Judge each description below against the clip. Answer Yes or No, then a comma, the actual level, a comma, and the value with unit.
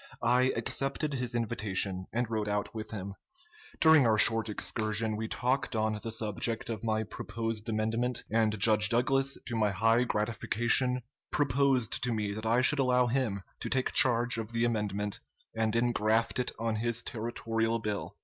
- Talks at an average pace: Yes, average, 165 wpm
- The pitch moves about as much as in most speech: No, narrow, 2.2 semitones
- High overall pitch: No, low, 115 Hz